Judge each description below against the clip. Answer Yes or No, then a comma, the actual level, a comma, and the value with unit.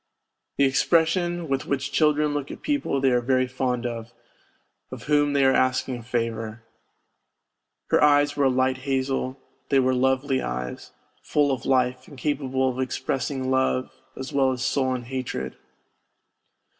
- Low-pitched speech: Yes, low, 130 Hz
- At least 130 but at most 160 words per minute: Yes, average, 155 wpm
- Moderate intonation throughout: No, narrow, 1.7 semitones